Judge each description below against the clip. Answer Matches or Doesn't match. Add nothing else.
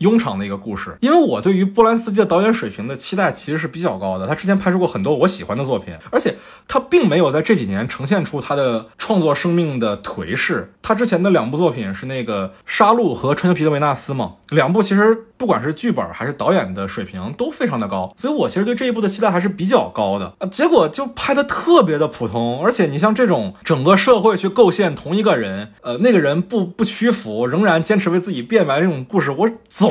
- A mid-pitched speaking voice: Matches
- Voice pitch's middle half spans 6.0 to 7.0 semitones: Matches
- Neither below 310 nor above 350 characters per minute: Doesn't match